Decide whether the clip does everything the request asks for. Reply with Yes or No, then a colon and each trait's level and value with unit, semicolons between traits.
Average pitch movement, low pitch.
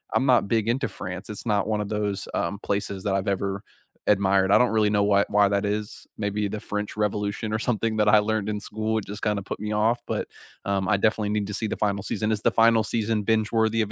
No: narrow, 1.4 semitones; low, 105 Hz